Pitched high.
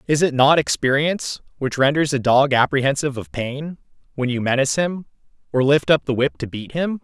No: low, 135 Hz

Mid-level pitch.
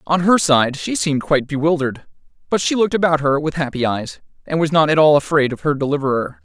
Yes: medium, 155 Hz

